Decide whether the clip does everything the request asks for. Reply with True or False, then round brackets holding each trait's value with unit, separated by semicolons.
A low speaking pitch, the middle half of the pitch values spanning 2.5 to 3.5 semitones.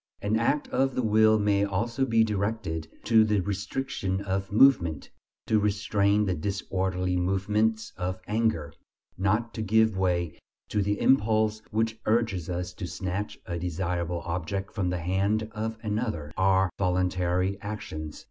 True (100 Hz; 3.1 semitones)